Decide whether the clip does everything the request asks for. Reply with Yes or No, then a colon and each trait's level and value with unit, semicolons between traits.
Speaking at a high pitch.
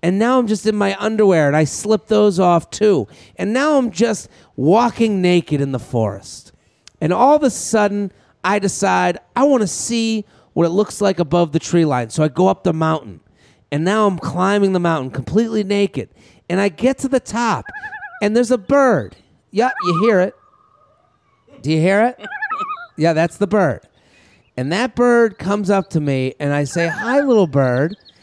Yes: high, 195 Hz